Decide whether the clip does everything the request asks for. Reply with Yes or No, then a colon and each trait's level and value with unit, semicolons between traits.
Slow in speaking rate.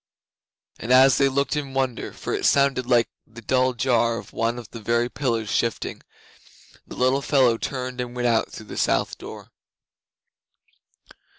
No: average, 160 wpm